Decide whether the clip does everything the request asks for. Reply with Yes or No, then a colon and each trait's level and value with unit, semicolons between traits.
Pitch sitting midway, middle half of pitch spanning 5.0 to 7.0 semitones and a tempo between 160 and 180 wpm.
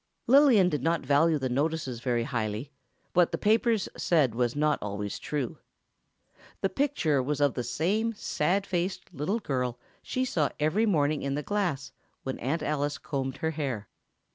Yes: medium, 150 Hz; wide, 5.4 semitones; average, 165 wpm